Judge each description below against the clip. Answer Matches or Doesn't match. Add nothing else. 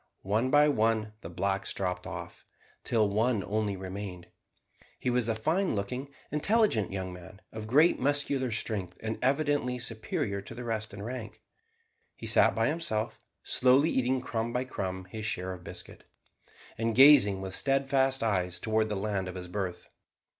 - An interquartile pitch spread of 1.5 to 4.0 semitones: Doesn't match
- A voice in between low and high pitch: Doesn't match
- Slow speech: Doesn't match